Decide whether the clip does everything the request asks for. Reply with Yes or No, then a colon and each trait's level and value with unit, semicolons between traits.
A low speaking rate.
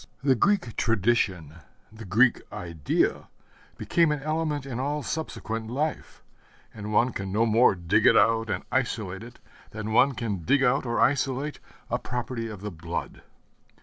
No: average, 155 wpm